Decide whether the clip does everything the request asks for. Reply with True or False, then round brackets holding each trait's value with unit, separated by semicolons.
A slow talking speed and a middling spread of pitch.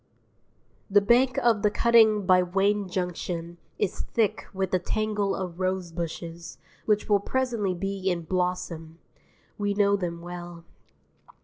True (130 wpm; 3.0 semitones)